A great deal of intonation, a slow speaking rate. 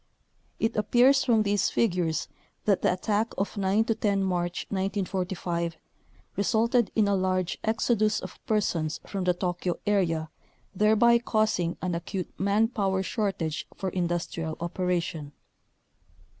No: average, 3.5 semitones; slow, 130 wpm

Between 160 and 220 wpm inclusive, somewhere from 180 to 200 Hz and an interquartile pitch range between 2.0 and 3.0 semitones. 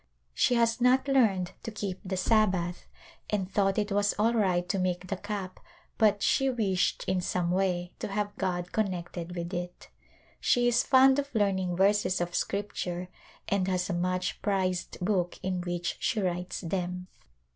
Yes: average, 165 wpm; high, 190 Hz; average, 2.7 semitones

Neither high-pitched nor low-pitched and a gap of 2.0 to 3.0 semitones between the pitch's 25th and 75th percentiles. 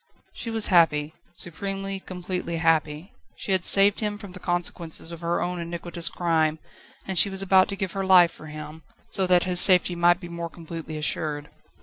Yes: medium, 175 Hz; narrow, 2.5 semitones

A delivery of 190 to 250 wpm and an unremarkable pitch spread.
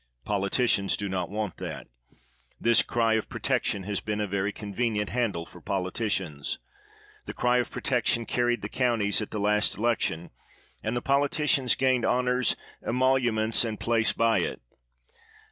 No: average, 145 wpm; average, 3.2 semitones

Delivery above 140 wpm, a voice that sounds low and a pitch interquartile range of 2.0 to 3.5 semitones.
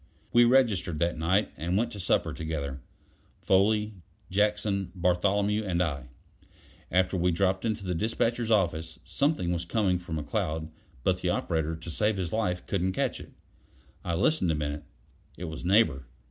No: average, 160 wpm; very low, 90 Hz; average, 4.2 semitones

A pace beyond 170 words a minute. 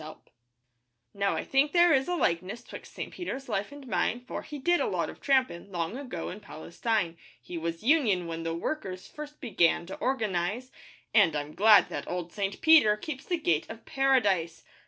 Yes: average, 195 wpm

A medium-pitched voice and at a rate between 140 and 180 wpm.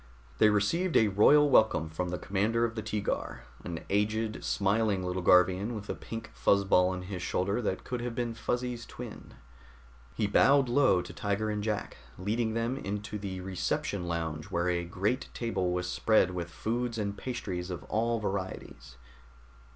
No: low, 105 Hz; average, 170 wpm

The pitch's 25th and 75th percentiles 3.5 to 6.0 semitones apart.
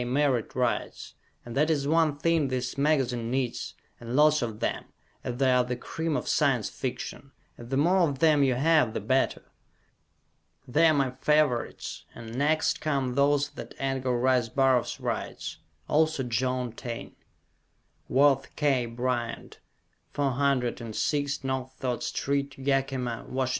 No: average, 2.8 semitones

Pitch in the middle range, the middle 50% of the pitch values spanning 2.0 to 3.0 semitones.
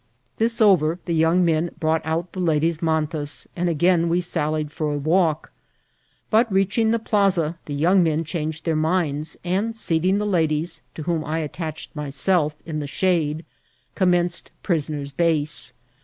Yes: medium, 165 Hz; average, 2.7 semitones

